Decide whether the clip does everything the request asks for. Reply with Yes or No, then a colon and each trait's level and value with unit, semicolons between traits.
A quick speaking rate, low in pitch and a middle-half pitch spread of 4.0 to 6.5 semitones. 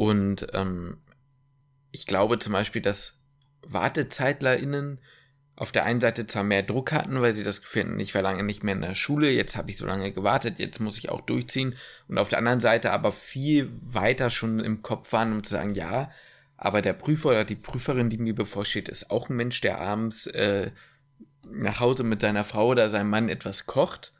Yes: fast, 200 wpm; low, 115 Hz; average, 4.7 semitones